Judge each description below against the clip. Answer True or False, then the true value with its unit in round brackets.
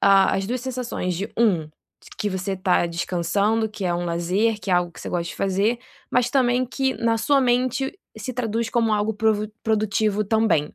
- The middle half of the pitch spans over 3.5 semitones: True (4.0 semitones)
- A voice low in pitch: False (215 Hz)